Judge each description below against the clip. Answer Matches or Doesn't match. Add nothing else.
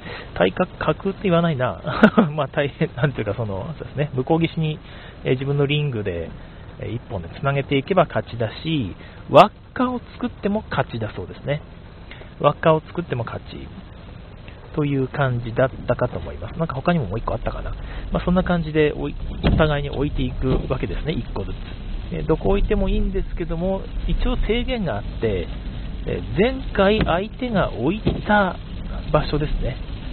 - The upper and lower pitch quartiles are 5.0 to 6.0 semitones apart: Doesn't match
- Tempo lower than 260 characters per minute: Doesn't match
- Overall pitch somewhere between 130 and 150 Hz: Matches